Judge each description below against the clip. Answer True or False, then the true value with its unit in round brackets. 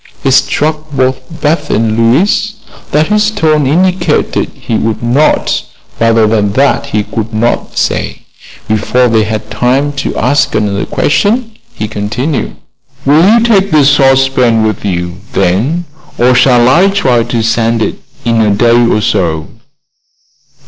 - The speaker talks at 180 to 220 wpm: False (145 wpm)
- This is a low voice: True (125 Hz)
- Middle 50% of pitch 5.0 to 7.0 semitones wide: True (5.6 semitones)